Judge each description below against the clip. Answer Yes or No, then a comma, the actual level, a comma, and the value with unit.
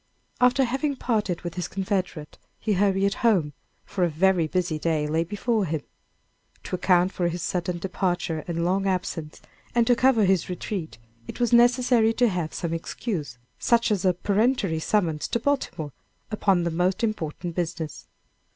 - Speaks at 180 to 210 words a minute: No, average, 160 wpm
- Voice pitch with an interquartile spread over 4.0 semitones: Yes, average, 4.6 semitones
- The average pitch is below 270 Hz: Yes, medium, 185 Hz